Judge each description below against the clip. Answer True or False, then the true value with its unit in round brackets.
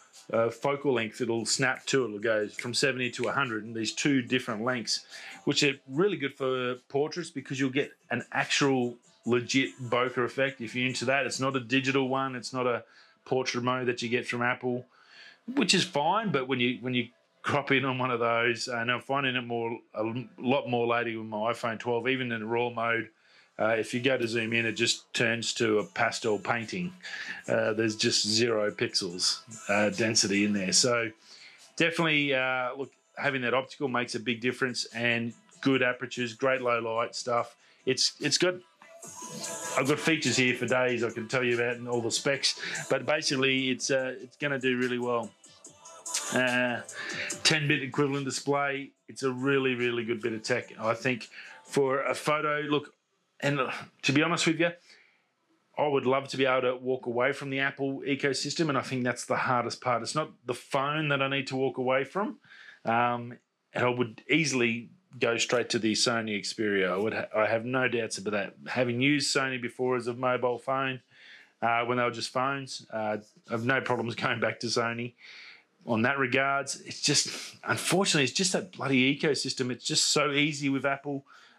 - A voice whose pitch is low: True (125 Hz)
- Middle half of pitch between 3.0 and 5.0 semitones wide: False (2.5 semitones)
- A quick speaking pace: False (195 wpm)